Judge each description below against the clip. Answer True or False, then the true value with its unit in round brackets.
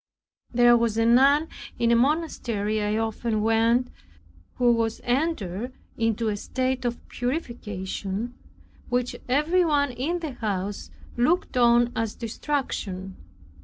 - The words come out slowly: True (125 wpm)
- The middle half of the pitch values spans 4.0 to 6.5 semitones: False (3.0 semitones)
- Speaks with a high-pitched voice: True (240 Hz)